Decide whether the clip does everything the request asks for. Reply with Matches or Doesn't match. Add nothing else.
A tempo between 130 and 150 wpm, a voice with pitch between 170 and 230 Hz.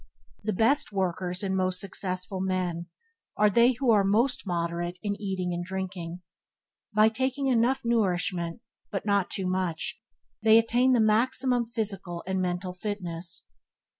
Matches